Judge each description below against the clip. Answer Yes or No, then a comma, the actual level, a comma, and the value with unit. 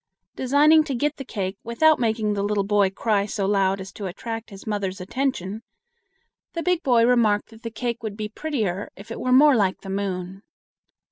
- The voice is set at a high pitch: Yes, high, 215 Hz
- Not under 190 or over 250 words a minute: Yes, average, 195 wpm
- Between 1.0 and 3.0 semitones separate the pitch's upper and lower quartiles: No, average, 4.0 semitones